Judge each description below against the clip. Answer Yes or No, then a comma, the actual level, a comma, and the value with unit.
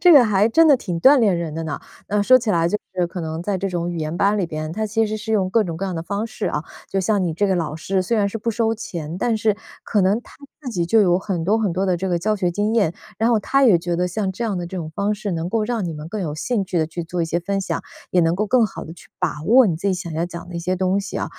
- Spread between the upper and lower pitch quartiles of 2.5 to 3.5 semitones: No, average, 4.0 semitones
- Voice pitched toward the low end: No, high, 190 Hz